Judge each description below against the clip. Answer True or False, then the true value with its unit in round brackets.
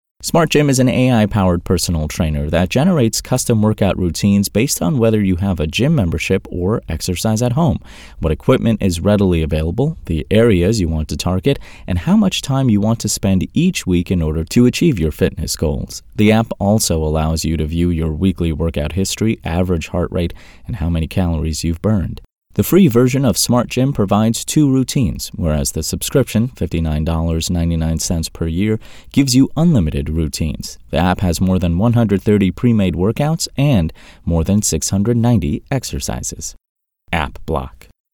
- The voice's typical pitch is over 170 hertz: False (95 Hz)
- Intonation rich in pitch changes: True (5.8 semitones)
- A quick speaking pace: False (175 wpm)